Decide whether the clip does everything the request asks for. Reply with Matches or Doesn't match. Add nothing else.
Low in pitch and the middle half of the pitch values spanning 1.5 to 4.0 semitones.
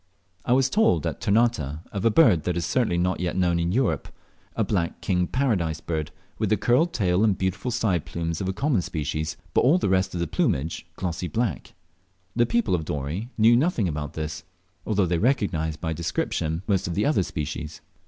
Doesn't match